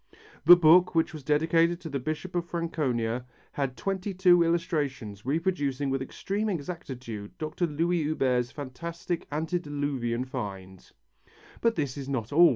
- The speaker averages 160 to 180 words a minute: No, average, 140 wpm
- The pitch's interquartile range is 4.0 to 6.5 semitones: Yes, average, 4.7 semitones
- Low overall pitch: No, medium, 150 Hz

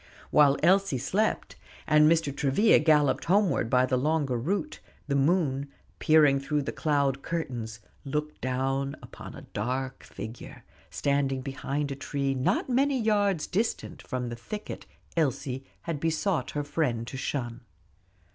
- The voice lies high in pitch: No, medium, 140 Hz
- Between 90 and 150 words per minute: Yes, average, 140 wpm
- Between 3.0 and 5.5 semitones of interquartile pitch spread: Yes, average, 3.7 semitones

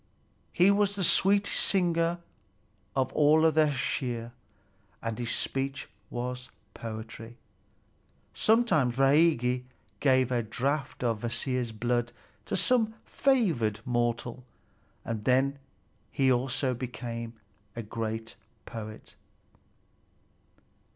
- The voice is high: No, low, 125 Hz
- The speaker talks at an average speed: No, slow, 95 wpm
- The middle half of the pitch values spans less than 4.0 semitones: No, average, 4.5 semitones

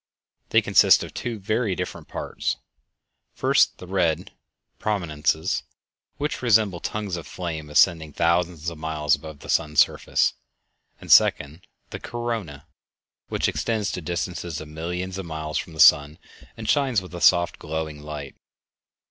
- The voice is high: No, very low, 85 Hz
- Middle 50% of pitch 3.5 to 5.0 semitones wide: Yes, average, 3.9 semitones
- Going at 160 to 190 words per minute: No, average, 140 wpm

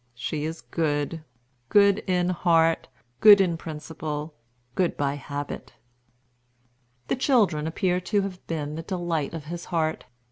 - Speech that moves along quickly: No, slow, 135 wpm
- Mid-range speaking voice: Yes, medium, 165 Hz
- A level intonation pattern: No, average, 3.2 semitones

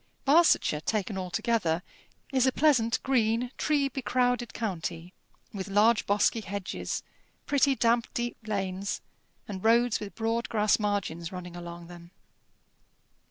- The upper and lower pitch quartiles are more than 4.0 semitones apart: Yes, average, 4.4 semitones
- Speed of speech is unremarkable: No, slow, 120 wpm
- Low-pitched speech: No, high, 215 Hz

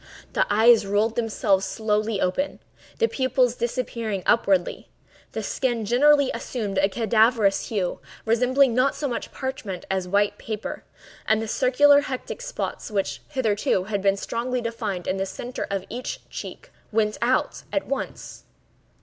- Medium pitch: No, high, 225 Hz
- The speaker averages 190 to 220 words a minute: No, average, 145 wpm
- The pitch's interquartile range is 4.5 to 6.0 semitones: No, average, 4.0 semitones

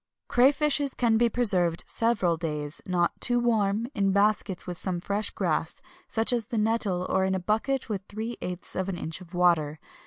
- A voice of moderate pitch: No, high, 195 Hz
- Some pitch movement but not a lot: Yes, average, 4.3 semitones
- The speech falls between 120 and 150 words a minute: No, average, 195 wpm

